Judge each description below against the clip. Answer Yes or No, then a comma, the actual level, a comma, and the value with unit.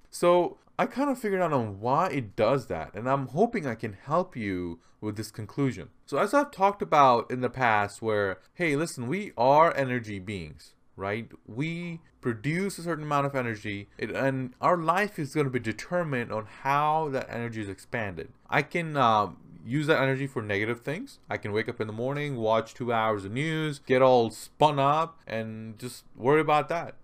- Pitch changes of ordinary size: No, wide, 5.7 semitones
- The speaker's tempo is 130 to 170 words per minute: No, average, 195 wpm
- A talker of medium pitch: No, low, 130 Hz